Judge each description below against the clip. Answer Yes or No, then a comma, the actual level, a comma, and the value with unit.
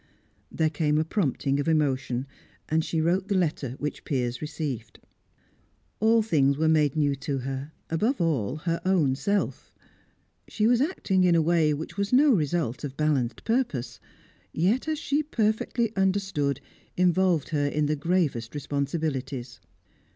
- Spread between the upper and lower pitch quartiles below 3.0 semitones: No, average, 5.2 semitones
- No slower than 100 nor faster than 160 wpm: Yes, average, 150 wpm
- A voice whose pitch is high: No, medium, 155 Hz